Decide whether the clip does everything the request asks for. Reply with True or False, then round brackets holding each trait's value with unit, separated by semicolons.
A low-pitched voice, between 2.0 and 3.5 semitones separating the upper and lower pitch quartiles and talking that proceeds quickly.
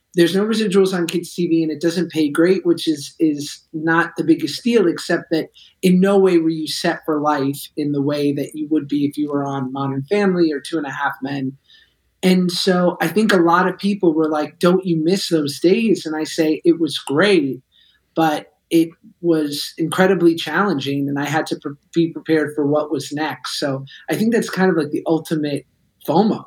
False (160 Hz; 3.1 semitones; 215 wpm)